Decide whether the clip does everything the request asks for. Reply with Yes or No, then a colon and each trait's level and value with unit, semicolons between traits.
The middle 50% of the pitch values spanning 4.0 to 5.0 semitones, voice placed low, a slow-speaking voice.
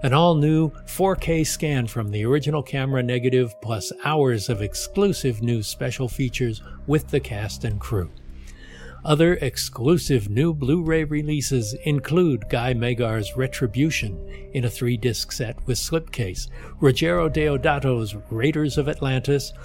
Yes: average, 4.4 semitones; low, 130 Hz; slow, 125 wpm